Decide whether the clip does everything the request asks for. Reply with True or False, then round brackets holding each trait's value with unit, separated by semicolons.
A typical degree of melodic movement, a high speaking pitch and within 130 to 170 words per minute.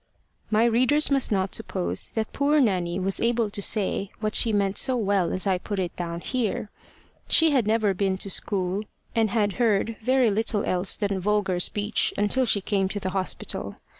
False (3.1 semitones; 205 Hz; 190 wpm)